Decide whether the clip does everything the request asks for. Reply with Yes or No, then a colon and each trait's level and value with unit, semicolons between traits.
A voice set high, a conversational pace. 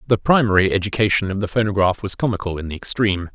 No: low, 100 Hz; average, 195 wpm